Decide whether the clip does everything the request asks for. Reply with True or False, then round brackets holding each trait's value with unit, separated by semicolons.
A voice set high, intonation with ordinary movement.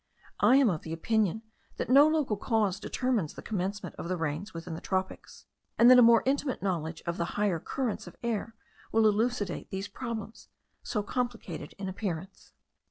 True (205 Hz; 4.7 semitones)